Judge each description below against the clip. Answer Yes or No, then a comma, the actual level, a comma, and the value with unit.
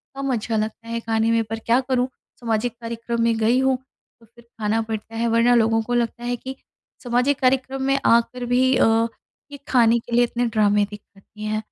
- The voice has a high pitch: Yes, high, 235 Hz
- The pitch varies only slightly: Yes, narrow, 1.7 semitones